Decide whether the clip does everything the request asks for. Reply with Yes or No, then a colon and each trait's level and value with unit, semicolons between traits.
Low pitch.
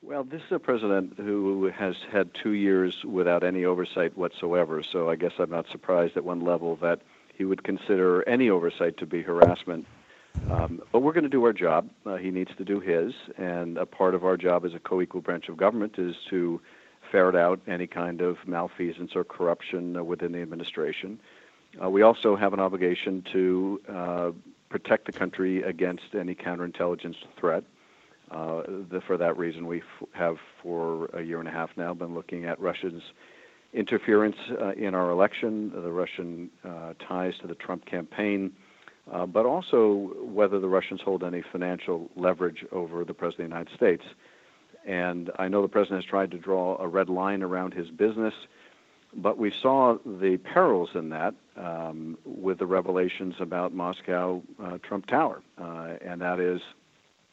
Yes: very low, 90 Hz